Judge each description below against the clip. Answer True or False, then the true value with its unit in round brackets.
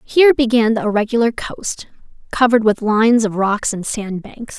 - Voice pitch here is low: False (225 Hz)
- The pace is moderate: True (155 wpm)